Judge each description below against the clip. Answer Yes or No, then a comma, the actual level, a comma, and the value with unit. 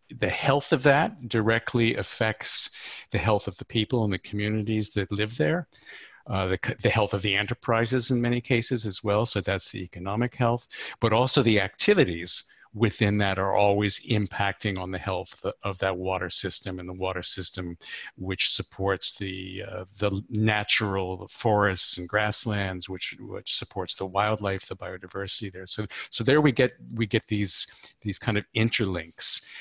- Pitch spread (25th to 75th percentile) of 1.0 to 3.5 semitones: Yes, average, 3.1 semitones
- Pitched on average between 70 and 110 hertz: Yes, low, 105 Hz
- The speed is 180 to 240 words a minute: No, average, 170 wpm